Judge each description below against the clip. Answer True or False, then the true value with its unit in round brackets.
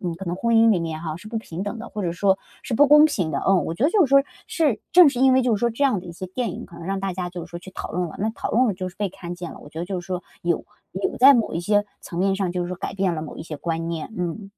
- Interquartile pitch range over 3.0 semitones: True (4.7 semitones)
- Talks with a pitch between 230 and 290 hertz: False (190 Hz)